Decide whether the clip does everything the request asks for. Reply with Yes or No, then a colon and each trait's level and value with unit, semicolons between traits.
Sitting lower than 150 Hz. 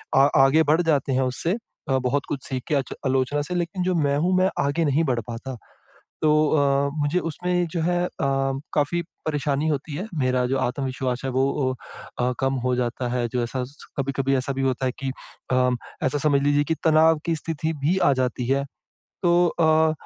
Yes: medium, 140 Hz